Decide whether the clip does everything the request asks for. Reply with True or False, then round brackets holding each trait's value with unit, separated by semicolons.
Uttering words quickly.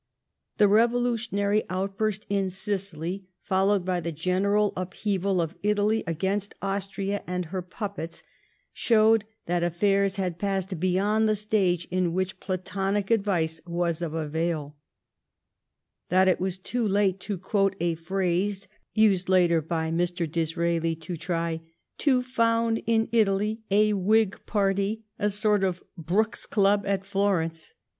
False (135 wpm)